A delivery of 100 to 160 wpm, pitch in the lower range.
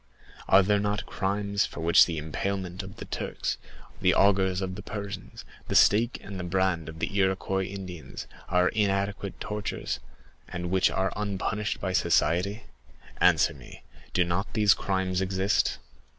Yes: average, 150 wpm; very low, 95 Hz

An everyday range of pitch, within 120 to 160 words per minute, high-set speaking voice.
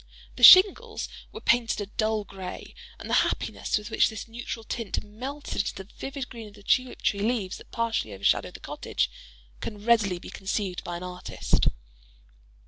No: average, 3.3 semitones; average, 175 wpm; high, 215 Hz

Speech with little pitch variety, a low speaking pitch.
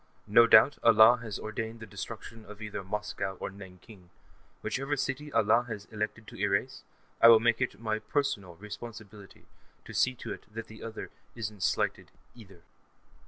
Yes: narrow, 2.3 semitones; low, 110 Hz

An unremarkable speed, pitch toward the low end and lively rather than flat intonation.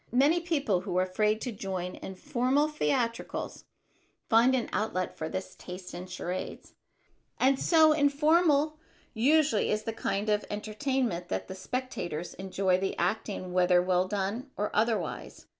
No: average, 145 wpm; high, 215 Hz; wide, 6.5 semitones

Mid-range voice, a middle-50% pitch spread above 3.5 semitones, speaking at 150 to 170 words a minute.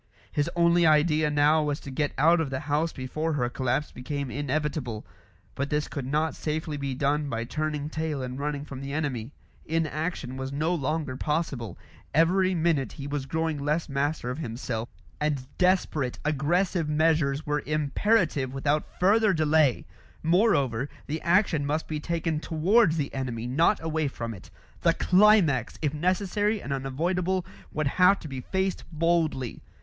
No: medium, 150 Hz; average, 3.1 semitones; average, 160 wpm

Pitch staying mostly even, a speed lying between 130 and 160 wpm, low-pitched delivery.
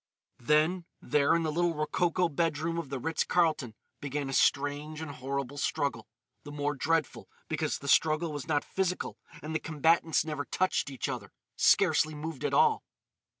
No: narrow, 2.3 semitones; average, 155 wpm; medium, 150 Hz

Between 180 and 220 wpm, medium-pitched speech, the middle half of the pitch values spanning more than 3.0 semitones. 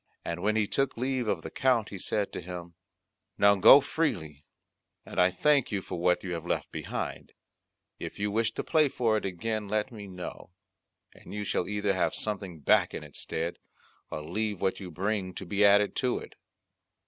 No: average, 195 wpm; low, 100 Hz; average, 3.4 semitones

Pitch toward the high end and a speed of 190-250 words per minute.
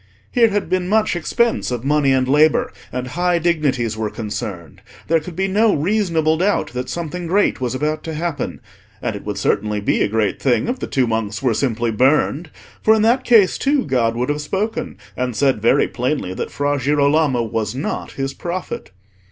No: medium, 145 Hz; average, 195 wpm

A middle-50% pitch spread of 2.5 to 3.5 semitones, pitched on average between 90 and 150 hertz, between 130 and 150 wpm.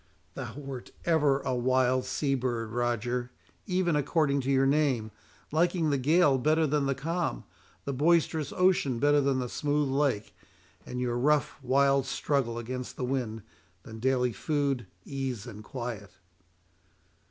Yes: average, 3.0 semitones; low, 135 Hz; average, 145 wpm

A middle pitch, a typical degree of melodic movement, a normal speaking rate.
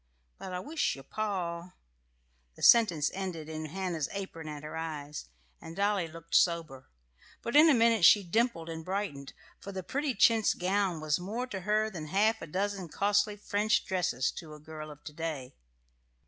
Yes: medium, 175 Hz; average, 5.0 semitones; average, 180 wpm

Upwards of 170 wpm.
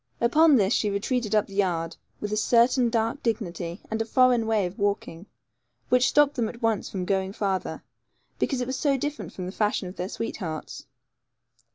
Yes: average, 190 wpm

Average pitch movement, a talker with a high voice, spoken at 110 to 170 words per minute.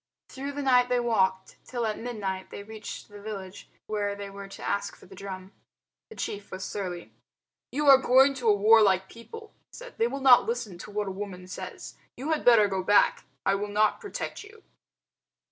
No: average, 4.1 semitones; high, 210 Hz; average, 200 wpm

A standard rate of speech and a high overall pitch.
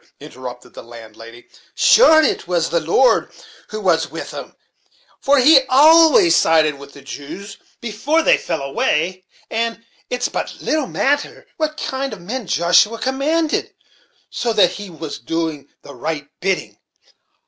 Yes: average, 145 wpm; high, 195 Hz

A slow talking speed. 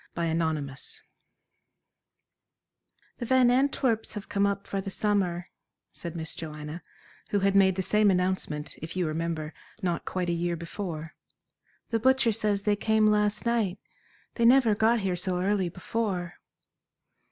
No: average, 145 wpm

